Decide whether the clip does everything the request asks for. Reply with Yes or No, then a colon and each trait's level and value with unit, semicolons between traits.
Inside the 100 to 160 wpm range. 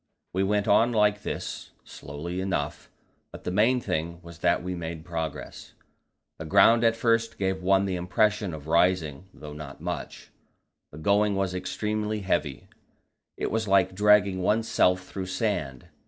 Yes: average, 155 wpm